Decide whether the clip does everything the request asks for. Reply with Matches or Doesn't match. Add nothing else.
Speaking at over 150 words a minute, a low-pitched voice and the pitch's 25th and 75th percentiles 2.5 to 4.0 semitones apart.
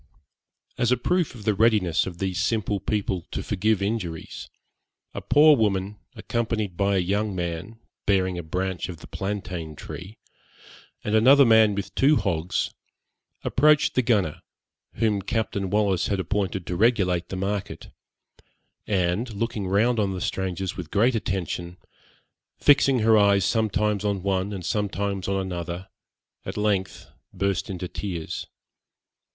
Doesn't match